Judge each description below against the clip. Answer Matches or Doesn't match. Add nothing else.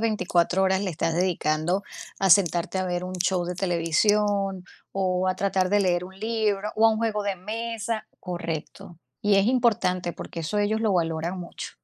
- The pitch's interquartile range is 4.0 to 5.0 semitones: Doesn't match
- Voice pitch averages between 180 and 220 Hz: Matches